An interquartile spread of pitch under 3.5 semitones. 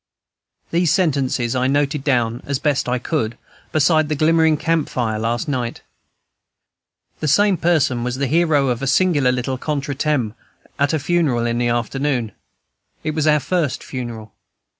No: average, 4.1 semitones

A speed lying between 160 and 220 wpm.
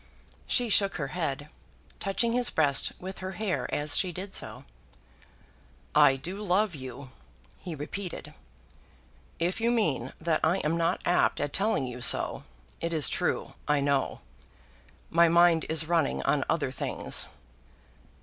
No: average, 145 wpm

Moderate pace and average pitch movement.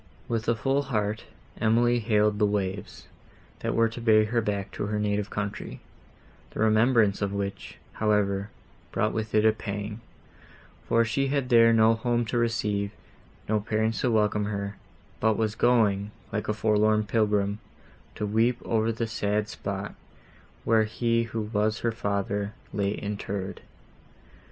No: average, 150 wpm; narrow, 1.9 semitones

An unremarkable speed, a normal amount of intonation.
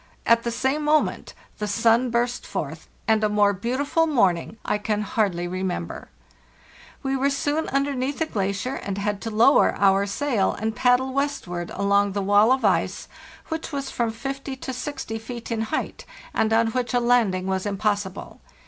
Yes: average, 170 wpm; average, 4.6 semitones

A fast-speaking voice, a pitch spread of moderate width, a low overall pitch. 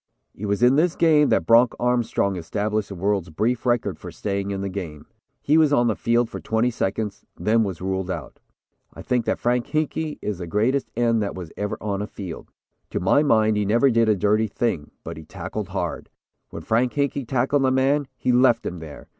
Yes: fast, 210 wpm; average, 4.0 semitones; low, 110 Hz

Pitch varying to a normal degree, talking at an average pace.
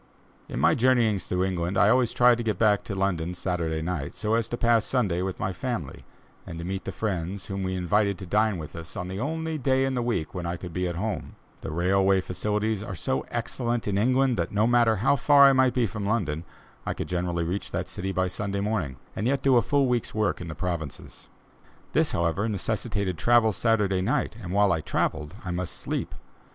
No: average, 4.6 semitones; fast, 220 wpm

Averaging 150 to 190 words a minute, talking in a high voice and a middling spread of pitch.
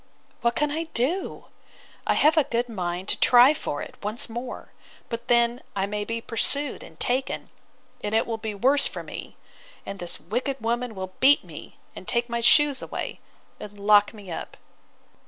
Yes: average, 175 wpm; high, 235 Hz; average, 4.0 semitones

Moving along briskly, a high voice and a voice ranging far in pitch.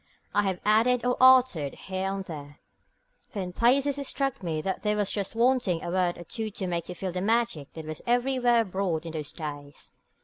Yes: fast, 210 wpm; high, 195 Hz; wide, 5.8 semitones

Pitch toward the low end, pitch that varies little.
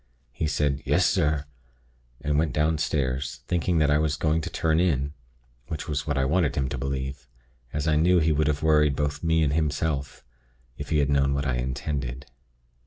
Yes: very low, 75 Hz; narrow, 2.2 semitones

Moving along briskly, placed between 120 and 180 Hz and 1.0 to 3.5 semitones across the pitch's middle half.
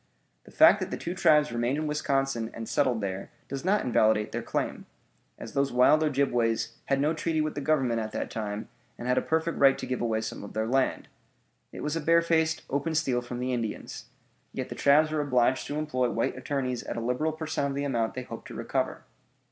No: fast, 220 wpm; low, 135 Hz; average, 4.3 semitones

